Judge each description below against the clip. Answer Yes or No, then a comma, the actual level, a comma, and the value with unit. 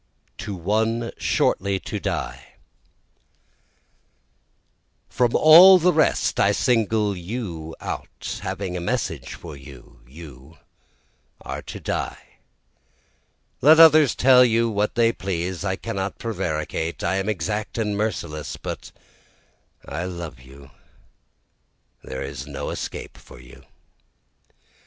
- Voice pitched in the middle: No, very low, 95 Hz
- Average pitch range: No, wide, 6.2 semitones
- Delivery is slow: Yes, slow, 115 wpm